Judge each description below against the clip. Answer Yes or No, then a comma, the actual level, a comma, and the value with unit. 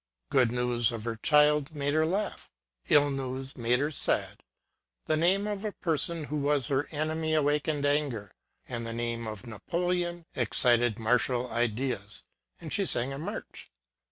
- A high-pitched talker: No, medium, 140 Hz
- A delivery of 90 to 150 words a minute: No, average, 160 wpm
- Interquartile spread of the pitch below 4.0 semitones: No, average, 4.6 semitones